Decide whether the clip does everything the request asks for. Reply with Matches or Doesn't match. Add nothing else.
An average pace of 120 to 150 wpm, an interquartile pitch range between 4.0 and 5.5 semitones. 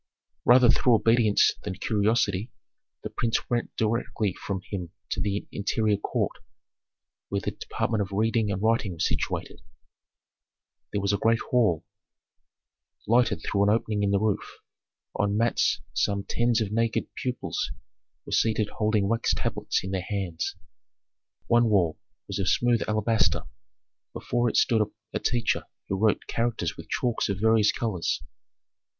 Doesn't match